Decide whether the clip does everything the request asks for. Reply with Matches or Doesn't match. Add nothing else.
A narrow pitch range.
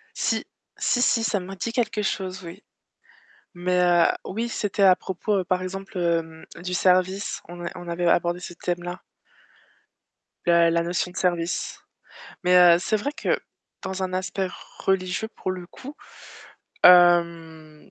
Matches